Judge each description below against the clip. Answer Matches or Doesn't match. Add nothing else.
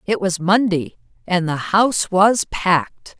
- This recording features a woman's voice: Matches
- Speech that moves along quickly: Doesn't match